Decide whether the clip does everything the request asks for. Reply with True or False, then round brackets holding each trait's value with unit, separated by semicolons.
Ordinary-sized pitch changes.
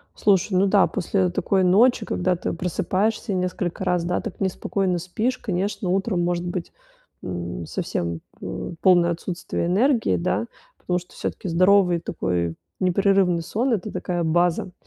False (2.3 semitones)